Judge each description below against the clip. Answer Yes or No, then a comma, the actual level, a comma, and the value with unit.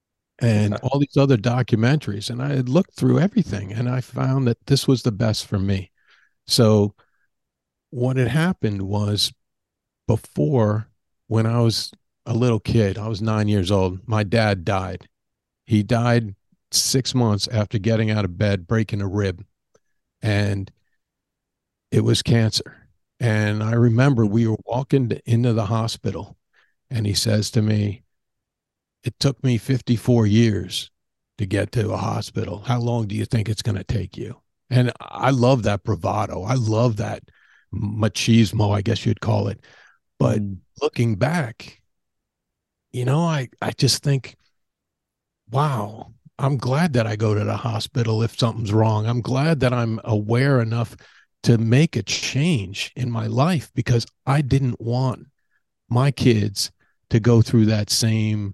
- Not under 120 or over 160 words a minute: Yes, average, 155 wpm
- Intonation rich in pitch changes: No, average, 3.1 semitones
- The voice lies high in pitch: No, low, 115 Hz